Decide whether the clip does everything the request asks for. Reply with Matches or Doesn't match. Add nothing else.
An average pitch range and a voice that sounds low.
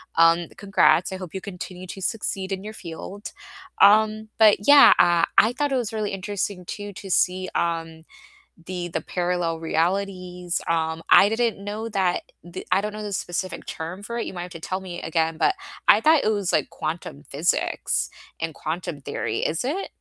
Doesn't match